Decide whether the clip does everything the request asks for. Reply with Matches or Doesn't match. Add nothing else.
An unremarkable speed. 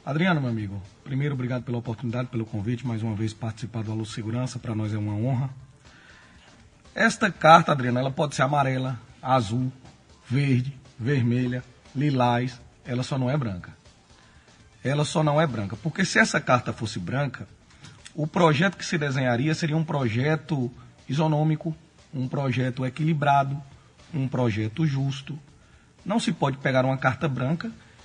Matches